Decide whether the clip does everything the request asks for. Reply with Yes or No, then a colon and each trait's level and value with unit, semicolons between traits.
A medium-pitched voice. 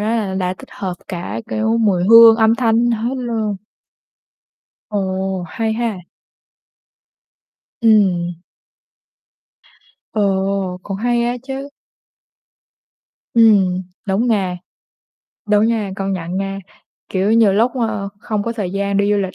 No: high, 205 Hz